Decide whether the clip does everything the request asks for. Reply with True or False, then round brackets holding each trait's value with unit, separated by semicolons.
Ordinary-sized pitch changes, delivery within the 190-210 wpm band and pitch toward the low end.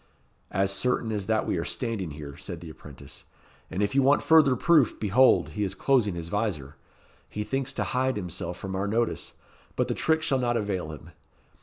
False (6.1 semitones; 195 wpm; 105 Hz)